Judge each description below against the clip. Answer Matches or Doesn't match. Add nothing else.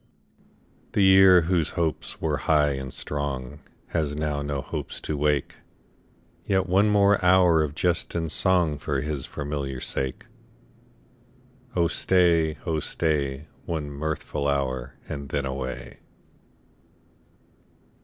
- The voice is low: Matches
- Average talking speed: Doesn't match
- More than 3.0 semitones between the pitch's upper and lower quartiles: Matches